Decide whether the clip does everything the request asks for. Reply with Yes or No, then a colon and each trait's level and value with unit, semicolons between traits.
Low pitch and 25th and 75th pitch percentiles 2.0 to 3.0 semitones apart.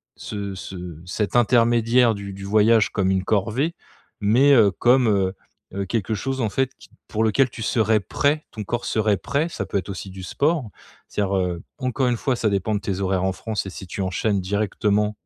No: low, 105 Hz; average, 3.5 semitones